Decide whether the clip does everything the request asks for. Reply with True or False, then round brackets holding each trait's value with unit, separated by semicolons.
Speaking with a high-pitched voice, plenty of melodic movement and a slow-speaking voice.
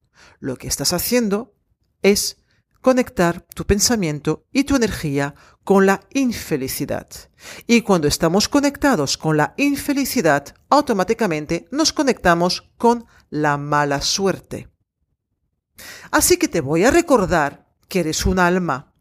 True (195 Hz; 8.3 semitones; 120 wpm)